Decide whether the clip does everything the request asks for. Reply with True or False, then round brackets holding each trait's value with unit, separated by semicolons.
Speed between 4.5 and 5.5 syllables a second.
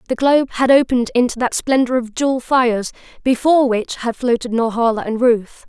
False (5.8 syllables/s)